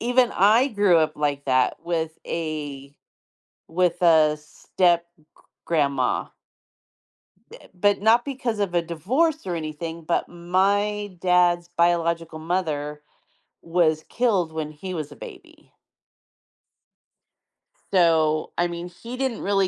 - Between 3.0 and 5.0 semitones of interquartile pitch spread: Yes, average, 3.9 semitones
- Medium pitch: Yes, medium, 170 Hz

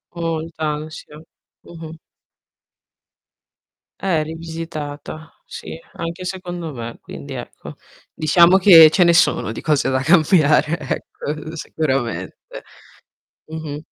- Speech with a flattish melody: Yes, narrow, 1.9 semitones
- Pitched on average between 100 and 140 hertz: No, medium, 160 Hz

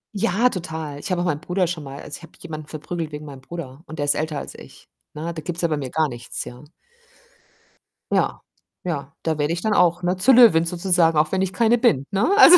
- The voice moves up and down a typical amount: Yes, average, 3.4 semitones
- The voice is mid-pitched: Yes, medium, 165 Hz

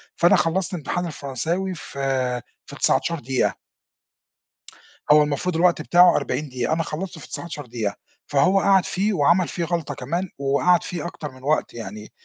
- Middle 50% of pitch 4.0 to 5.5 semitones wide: Yes, average, 4.5 semitones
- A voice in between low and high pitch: Yes, medium, 155 Hz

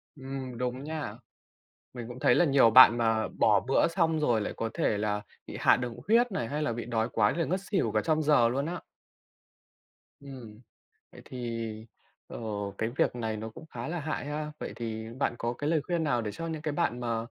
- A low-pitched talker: Yes, low, 125 Hz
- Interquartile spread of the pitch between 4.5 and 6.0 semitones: Yes, average, 5.1 semitones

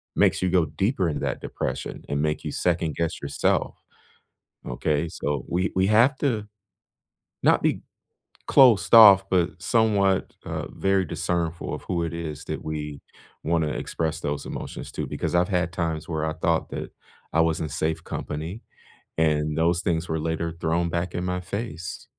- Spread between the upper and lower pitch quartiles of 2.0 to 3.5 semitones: Yes, average, 2.8 semitones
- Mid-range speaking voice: No, very low, 85 Hz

